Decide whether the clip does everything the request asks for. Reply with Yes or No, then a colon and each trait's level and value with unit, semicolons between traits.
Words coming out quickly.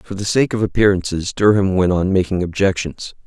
No: average, 185 wpm